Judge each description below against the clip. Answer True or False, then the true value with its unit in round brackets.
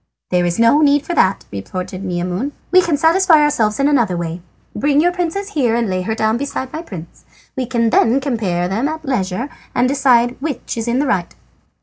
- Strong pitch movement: True (7.3 semitones)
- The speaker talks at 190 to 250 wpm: True (205 wpm)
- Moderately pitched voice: False (245 Hz)